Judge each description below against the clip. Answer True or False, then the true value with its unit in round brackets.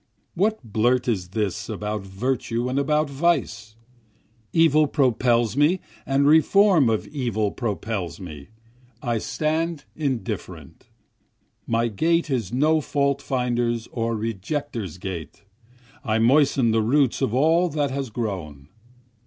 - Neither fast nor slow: False (120 wpm)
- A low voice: True (120 Hz)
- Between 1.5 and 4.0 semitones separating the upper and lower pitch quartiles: False (5.3 semitones)